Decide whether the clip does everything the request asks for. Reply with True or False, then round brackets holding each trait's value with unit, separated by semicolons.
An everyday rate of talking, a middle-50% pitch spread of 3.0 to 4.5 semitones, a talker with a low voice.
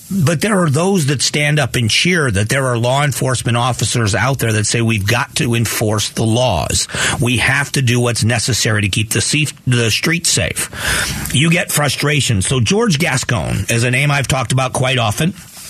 True (190 wpm; 3.9 semitones; 130 Hz)